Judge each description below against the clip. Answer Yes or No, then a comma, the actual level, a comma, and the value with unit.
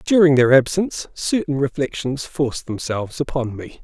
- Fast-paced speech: No, average, 140 wpm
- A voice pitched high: No, medium, 140 Hz